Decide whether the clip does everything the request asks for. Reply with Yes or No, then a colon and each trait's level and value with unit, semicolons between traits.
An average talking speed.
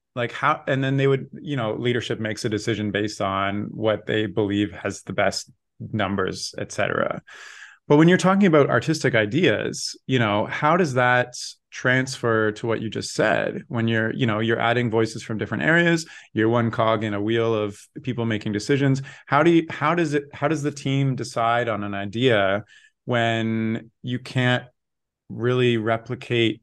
Yes: average, 180 wpm